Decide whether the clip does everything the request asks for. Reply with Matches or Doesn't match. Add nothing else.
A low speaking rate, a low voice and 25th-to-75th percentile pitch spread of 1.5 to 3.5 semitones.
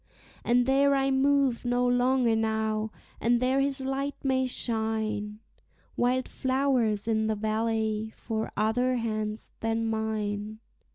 Doesn't match